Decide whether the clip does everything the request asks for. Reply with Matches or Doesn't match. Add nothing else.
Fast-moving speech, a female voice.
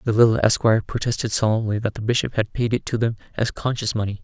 Doesn't match